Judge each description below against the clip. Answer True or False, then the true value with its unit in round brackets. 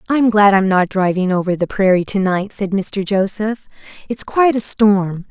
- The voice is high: True (200 Hz)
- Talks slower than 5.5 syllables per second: True (4.7 syllables/s)